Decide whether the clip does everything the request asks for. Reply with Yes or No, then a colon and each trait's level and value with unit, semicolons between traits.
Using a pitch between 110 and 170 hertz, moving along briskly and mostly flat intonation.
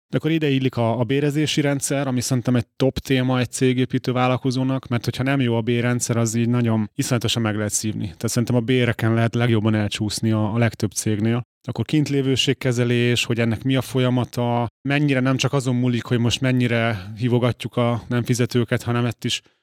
Yes: low, 120 Hz; fast, 190 wpm; narrow, 2.0 semitones